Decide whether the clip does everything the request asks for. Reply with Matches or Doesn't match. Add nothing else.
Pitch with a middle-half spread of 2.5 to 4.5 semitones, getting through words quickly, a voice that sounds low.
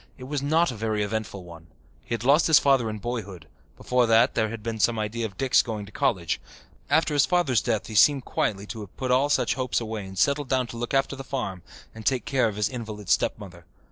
Matches